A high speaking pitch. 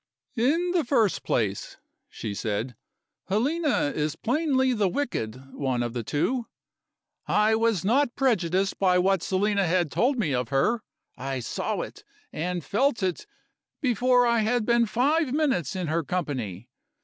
Yes: high, 200 Hz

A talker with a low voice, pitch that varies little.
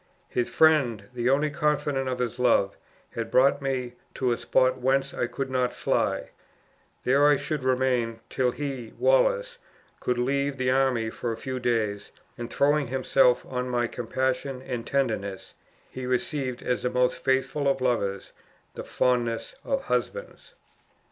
Yes: low, 130 Hz; narrow, 2.2 semitones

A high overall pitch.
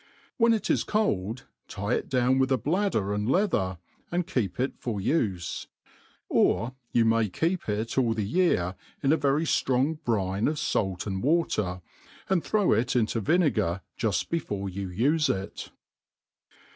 No: low, 120 Hz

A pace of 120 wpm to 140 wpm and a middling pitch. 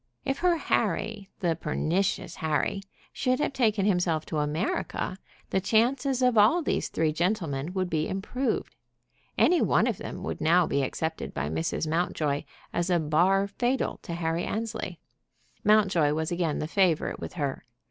No: average, 160 wpm; medium, 180 Hz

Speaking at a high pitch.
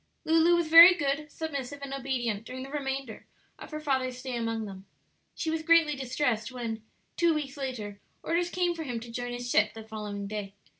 Yes: very high, 265 Hz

